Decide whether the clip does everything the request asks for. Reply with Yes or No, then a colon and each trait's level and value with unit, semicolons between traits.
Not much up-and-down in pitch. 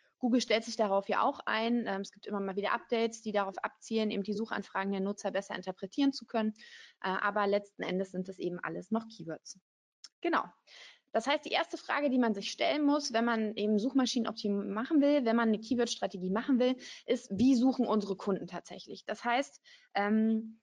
No: average, 3.7 semitones